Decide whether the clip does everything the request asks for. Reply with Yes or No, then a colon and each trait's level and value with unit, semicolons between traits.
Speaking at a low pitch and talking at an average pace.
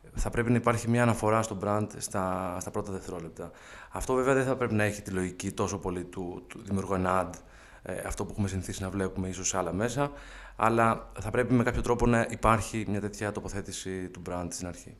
No: low, 100 Hz; fast, 215 wpm